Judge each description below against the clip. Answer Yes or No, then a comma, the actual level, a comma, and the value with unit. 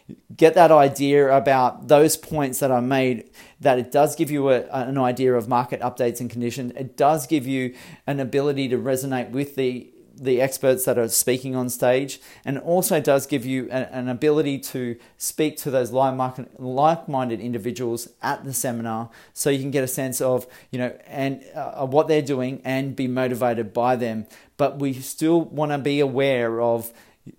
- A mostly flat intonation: Yes, narrow, 2.1 semitones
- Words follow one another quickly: No, average, 190 wpm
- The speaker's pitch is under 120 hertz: No, low, 130 Hz